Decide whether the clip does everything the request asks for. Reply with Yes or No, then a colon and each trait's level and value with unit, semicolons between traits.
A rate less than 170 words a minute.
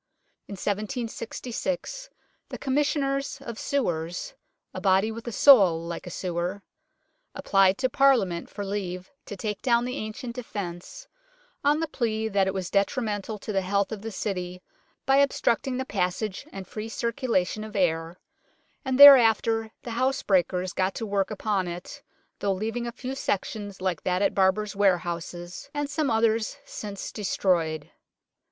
Yes: average, 155 wpm